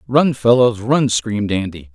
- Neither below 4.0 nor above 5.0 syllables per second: Yes, 4.5 syllables/s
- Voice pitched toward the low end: Yes, low, 115 Hz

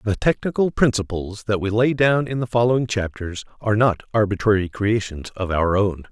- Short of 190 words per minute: Yes, average, 175 wpm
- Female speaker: No, male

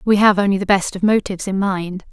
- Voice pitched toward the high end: Yes, high, 195 Hz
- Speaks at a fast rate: Yes, fast, 255 wpm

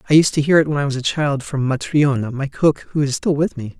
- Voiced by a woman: No, male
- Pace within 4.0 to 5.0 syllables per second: No, 6.0 syllables/s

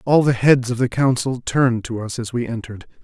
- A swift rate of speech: Yes, fast, 235 wpm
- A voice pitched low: Yes, low, 120 Hz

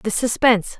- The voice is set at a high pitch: Yes, high, 225 Hz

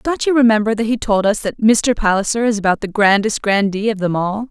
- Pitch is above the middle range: Yes, high, 215 Hz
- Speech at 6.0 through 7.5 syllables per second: No, 5.6 syllables/s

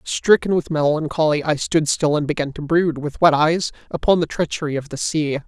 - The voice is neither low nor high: Yes, medium, 155 Hz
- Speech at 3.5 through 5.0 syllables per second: No, 5.3 syllables/s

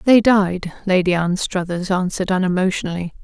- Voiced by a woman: Yes, female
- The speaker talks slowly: Yes, slow, 110 wpm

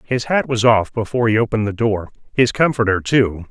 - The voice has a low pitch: Yes, low, 110 Hz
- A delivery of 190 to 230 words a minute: Yes, fast, 205 wpm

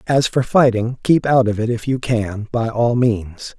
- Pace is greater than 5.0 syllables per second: No, 4.1 syllables/s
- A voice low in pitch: Yes, low, 120 Hz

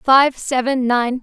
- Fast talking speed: No, average, 145 wpm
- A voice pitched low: No, very high, 255 Hz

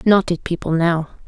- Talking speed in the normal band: Yes, average, 190 wpm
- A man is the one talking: No, female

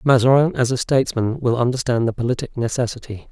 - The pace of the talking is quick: No, average, 165 wpm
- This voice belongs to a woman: No, male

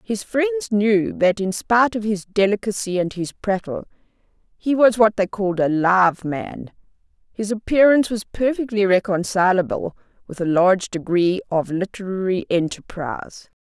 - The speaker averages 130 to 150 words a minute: Yes, average, 140 wpm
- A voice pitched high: Yes, high, 200 Hz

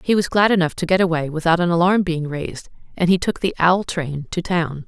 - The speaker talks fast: Yes, fast, 245 wpm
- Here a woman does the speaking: Yes, female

